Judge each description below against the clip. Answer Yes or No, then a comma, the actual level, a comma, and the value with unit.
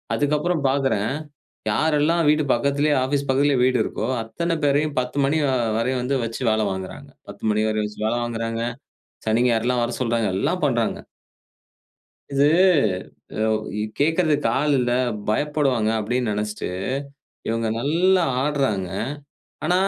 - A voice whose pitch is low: Yes, low, 130 Hz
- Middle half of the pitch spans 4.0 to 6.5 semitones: Yes, average, 4.6 semitones